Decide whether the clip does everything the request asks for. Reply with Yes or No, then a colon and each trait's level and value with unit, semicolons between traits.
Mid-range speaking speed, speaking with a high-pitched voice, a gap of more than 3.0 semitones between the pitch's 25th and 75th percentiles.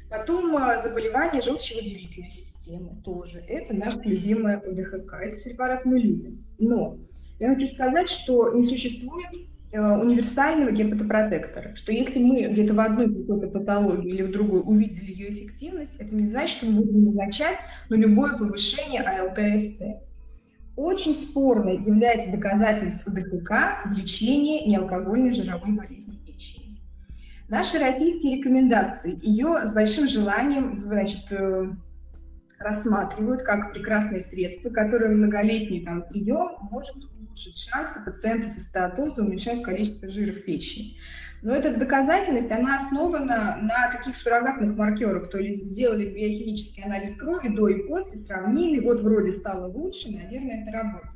Yes: average, 130 wpm; high, 215 Hz; average, 3.9 semitones